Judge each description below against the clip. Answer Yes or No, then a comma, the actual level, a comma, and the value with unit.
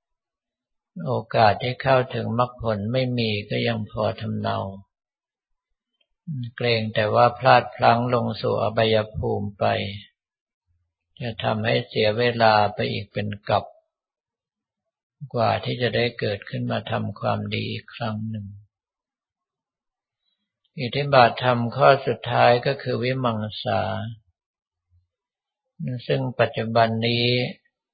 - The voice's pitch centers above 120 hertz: No, low, 115 Hz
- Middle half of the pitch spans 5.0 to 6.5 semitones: No, narrow, 2.6 semitones